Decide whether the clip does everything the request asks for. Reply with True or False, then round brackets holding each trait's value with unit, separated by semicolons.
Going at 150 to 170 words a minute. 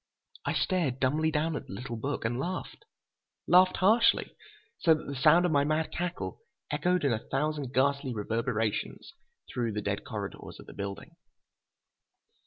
True (160 wpm)